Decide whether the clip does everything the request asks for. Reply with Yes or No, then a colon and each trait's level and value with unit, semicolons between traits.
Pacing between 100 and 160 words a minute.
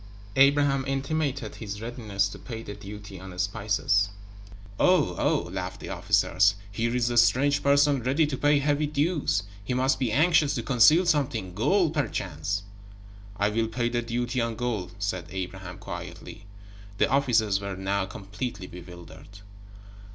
Yes: average, 150 wpm